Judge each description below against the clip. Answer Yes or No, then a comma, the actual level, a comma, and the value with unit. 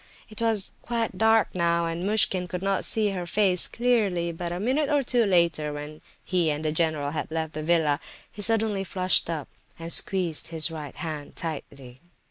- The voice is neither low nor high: Yes, medium, 175 Hz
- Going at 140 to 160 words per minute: No, average, 185 wpm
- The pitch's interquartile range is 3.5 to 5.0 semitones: Yes, average, 4.6 semitones